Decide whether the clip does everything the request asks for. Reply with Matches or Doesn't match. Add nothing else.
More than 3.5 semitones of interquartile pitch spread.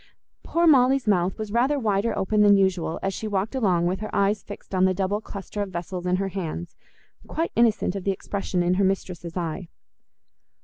Doesn't match